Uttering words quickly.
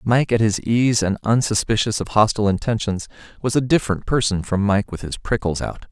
No: average, 195 wpm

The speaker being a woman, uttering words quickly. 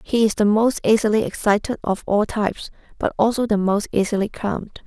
No: female; average, 185 wpm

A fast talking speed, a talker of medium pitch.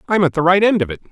Yes: fast, 375 wpm; medium, 175 Hz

